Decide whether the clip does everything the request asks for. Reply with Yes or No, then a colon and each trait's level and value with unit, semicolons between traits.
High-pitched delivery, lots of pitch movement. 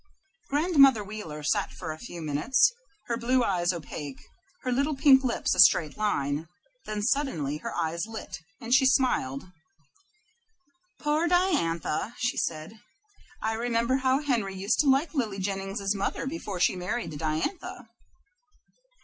Yes: high, 215 Hz; wide, 7.8 semitones